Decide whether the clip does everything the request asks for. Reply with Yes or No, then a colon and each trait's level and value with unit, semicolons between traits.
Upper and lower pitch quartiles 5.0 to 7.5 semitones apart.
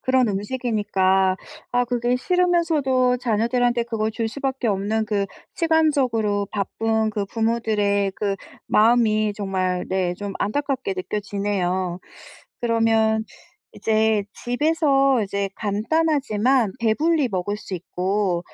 No: average, 3.8 semitones